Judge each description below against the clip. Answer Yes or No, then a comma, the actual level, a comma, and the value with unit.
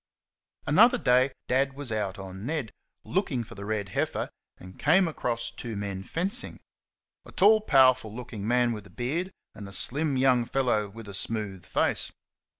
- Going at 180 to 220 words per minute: No, average, 165 wpm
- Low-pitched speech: Yes, low, 120 Hz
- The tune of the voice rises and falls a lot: No, average, 5.0 semitones